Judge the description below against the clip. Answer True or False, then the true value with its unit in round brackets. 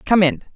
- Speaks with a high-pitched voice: True (195 Hz)